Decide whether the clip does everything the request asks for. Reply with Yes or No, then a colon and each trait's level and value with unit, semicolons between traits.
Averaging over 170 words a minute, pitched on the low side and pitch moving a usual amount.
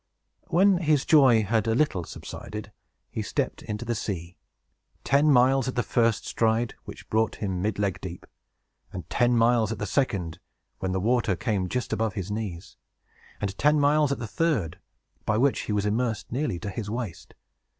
Yes: average, 180 wpm; low, 115 Hz; average, 3.9 semitones